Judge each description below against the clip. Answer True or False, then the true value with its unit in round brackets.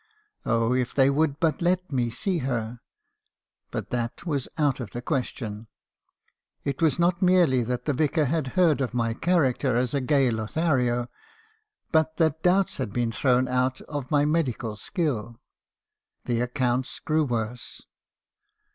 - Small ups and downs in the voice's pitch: False (4.6 semitones)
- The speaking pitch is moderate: False (130 Hz)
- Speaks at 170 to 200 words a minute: False (155 wpm)